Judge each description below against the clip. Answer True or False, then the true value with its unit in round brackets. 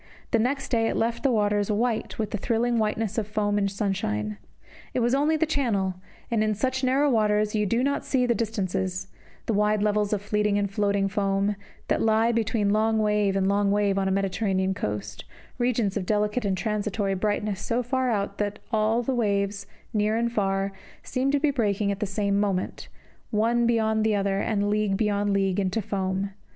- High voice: True (210 Hz)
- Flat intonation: True (2.3 semitones)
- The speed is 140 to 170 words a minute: False (195 wpm)